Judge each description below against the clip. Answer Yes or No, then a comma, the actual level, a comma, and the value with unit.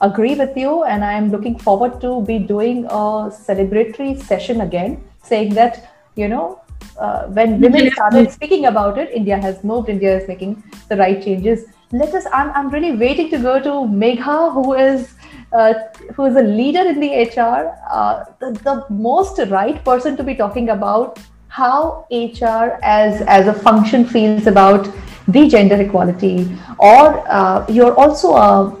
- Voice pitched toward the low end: No, high, 230 Hz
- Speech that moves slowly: No, average, 170 wpm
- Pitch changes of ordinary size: Yes, average, 4.5 semitones